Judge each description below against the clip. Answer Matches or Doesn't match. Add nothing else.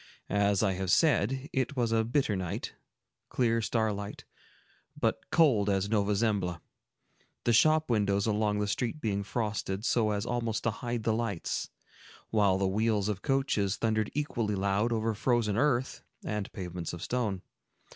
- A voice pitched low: Matches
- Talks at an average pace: Matches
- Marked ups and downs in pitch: Doesn't match